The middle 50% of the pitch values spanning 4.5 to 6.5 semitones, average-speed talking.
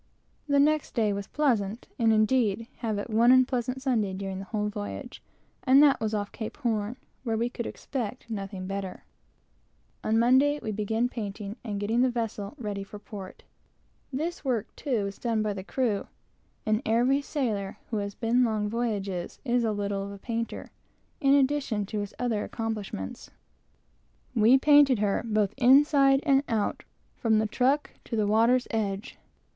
No: average, 3.7 semitones; average, 170 wpm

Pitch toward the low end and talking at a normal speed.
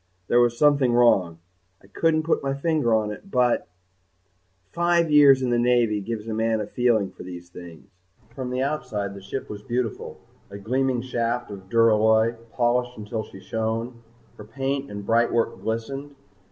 Yes: low, 120 Hz; average, 165 wpm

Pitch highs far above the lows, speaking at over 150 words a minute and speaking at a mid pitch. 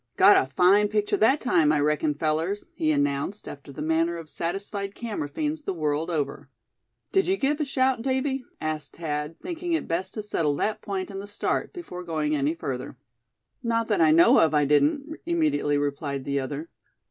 Yes: wide, 7.4 semitones; average, 190 wpm; medium, 170 Hz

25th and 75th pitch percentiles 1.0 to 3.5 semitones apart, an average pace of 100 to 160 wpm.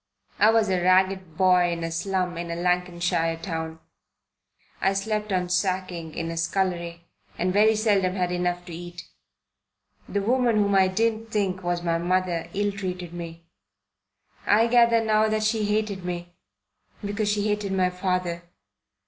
Yes: average, 2.9 semitones; average, 155 wpm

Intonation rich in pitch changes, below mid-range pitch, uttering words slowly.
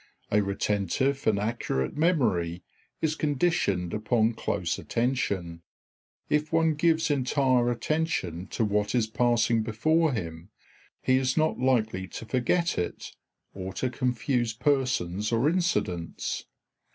Yes: wide, 6.0 semitones; low, 120 Hz; slow, 120 wpm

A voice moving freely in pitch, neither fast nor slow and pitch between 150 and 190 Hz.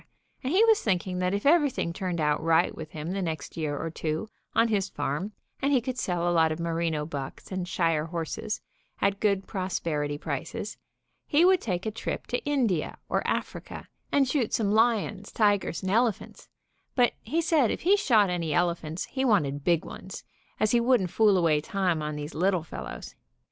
Yes: wide, 5.7 semitones; average, 190 wpm; medium, 185 Hz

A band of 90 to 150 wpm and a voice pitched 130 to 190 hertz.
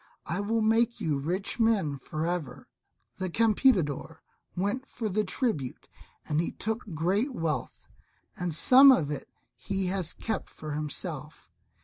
Yes: average, 140 wpm; medium, 185 Hz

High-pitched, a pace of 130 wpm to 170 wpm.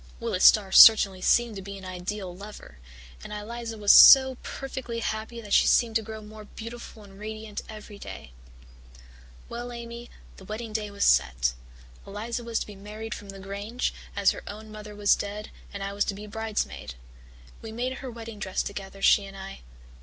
No: high, 210 Hz; average, 185 wpm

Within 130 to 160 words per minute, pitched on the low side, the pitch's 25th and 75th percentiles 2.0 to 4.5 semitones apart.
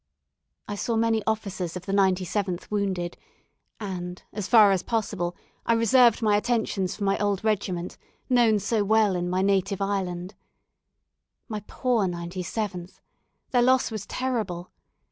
No: average, 140 wpm; high, 200 Hz; average, 3.3 semitones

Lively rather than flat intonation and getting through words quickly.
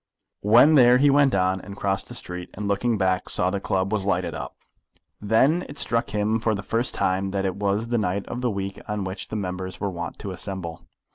No: average, 3.3 semitones; fast, 225 wpm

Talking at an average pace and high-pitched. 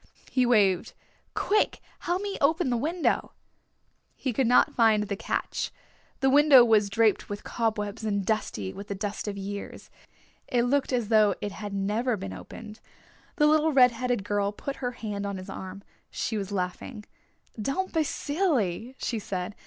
Yes: average, 170 wpm; high, 220 Hz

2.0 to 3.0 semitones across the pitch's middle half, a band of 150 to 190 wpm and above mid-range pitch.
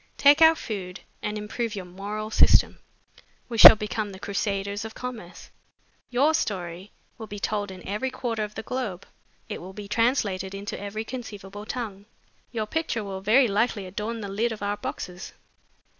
Yes: narrow, 2.6 semitones; average, 170 wpm; high, 210 Hz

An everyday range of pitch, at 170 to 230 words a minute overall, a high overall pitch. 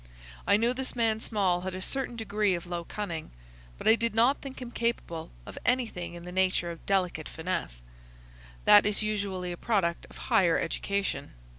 Yes: average, 4.5 semitones; average, 180 wpm; high, 200 Hz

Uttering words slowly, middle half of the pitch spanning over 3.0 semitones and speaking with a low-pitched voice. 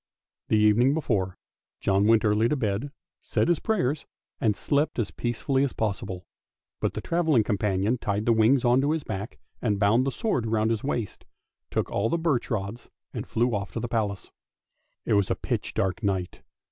No: average, 185 wpm; average, 4.4 semitones; low, 115 Hz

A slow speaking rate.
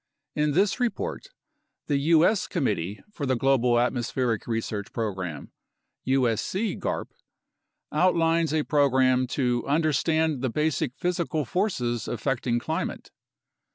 Yes: slow, 105 wpm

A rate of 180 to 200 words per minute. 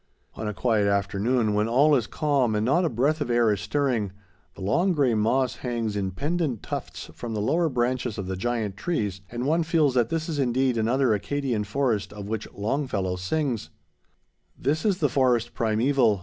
Yes: average, 190 wpm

